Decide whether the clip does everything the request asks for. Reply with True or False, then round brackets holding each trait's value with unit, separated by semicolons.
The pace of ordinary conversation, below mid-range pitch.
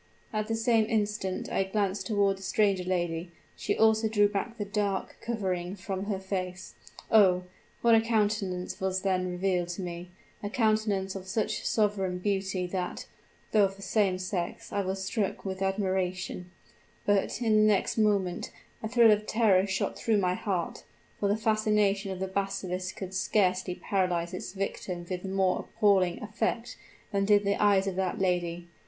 False (170 wpm; 195 Hz)